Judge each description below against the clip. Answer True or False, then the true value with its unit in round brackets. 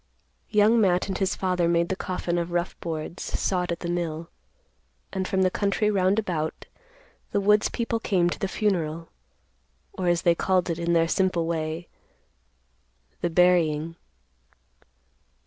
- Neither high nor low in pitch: True (175 Hz)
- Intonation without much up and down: True (2.1 semitones)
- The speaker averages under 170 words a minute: True (150 wpm)